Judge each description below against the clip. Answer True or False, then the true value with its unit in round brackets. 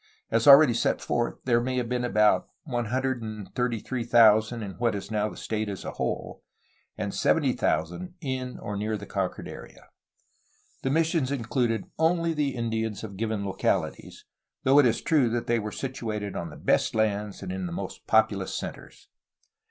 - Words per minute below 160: False (165 wpm)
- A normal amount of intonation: True (3.6 semitones)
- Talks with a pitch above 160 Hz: False (115 Hz)